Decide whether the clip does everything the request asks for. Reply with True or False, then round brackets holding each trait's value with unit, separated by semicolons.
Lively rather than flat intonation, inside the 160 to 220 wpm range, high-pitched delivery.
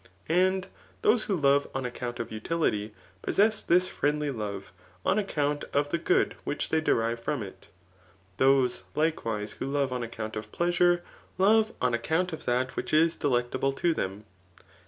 False (6.0 semitones; 165 wpm; 145 Hz)